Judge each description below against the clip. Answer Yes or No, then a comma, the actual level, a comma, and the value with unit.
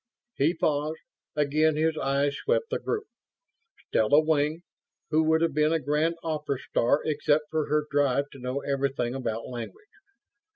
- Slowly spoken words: No, average, 155 wpm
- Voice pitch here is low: No, medium, 150 Hz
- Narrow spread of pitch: Yes, narrow, 2.3 semitones